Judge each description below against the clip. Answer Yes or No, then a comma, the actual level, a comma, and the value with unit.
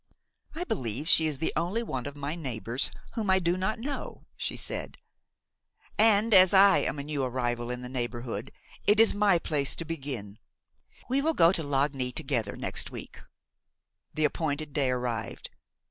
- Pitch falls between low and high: Yes, medium, 150 Hz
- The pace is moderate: Yes, average, 170 wpm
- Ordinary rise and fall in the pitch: No, wide, 7.0 semitones